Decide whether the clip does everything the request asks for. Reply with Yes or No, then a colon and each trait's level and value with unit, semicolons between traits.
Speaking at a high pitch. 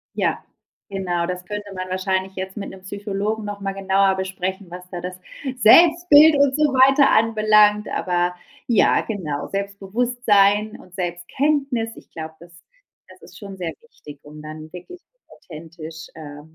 Yes: high, 195 Hz